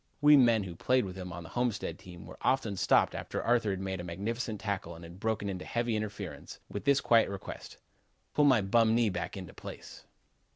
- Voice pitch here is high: No, low, 105 Hz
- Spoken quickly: Yes, fast, 210 wpm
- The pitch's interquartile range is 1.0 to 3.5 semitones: No, average, 4.1 semitones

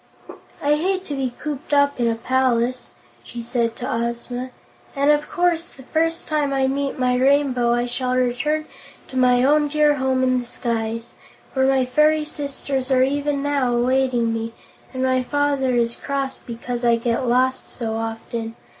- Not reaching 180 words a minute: Yes, average, 170 wpm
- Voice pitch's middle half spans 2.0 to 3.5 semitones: Yes, average, 2.9 semitones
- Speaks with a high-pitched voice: Yes, very high, 260 Hz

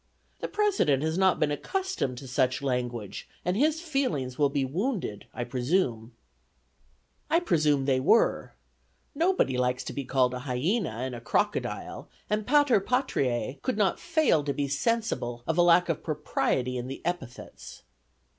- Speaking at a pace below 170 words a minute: Yes, average, 155 wpm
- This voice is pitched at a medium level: Yes, medium, 145 Hz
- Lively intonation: Yes, wide, 9.0 semitones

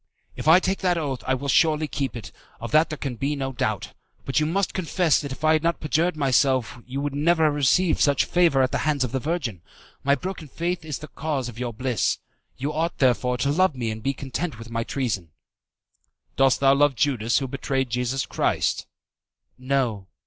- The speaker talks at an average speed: No, fast, 210 wpm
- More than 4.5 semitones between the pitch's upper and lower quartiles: No, average, 3.6 semitones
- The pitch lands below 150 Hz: Yes, medium, 140 Hz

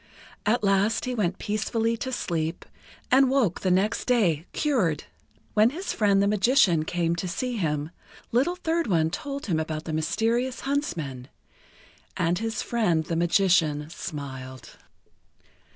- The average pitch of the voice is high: Yes, high, 195 Hz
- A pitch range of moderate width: No, wide, 6.6 semitones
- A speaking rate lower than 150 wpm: Yes, average, 140 wpm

